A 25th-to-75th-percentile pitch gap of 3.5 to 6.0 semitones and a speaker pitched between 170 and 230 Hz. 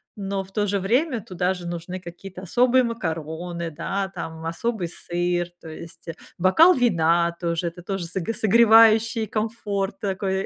Yes: average, 4.2 semitones; high, 190 Hz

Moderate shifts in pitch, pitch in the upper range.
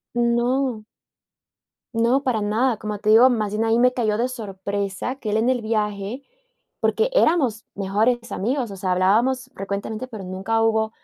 Yes: average, 3.3 semitones; high, 225 Hz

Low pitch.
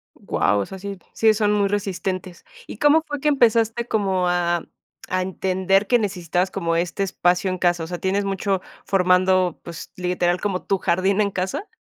No: high, 190 Hz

